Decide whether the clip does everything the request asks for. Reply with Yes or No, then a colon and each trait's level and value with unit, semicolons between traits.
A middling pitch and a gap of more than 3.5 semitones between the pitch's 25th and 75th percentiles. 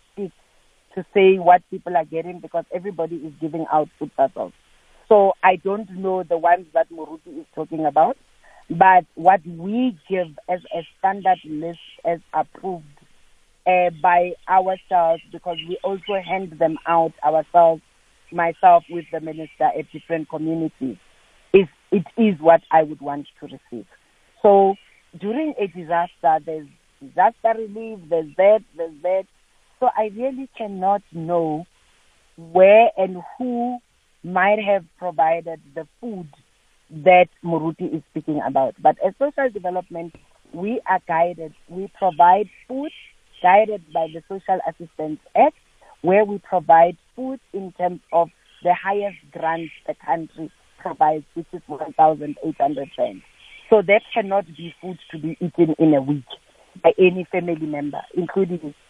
No: medium, 175 Hz; average, 3.2 semitones